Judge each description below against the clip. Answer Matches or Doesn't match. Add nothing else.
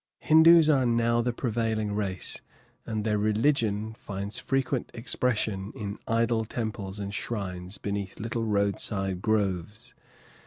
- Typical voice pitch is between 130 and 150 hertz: Doesn't match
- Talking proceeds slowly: Matches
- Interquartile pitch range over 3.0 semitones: Doesn't match